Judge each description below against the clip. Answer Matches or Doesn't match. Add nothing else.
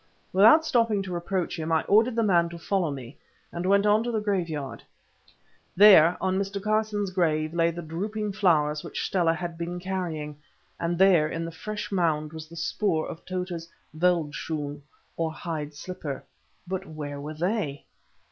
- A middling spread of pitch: Matches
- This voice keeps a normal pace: Matches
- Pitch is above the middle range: Doesn't match